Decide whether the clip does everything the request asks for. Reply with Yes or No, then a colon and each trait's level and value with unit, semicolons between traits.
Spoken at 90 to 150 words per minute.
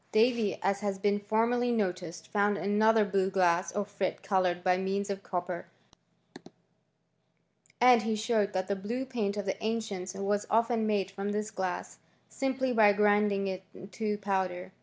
No: average, 160 wpm